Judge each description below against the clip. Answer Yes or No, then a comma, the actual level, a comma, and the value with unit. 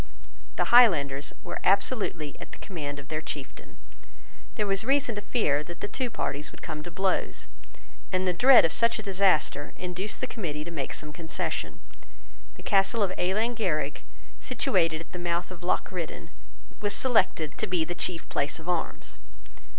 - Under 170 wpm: No, average, 175 wpm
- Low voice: No, medium, 180 Hz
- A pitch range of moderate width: Yes, average, 4.8 semitones